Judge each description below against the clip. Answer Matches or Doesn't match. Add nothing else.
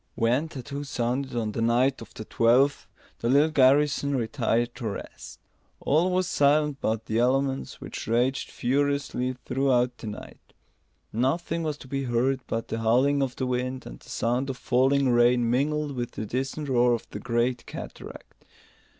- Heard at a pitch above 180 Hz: Doesn't match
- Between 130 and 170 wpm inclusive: Matches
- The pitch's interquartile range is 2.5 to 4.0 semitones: Matches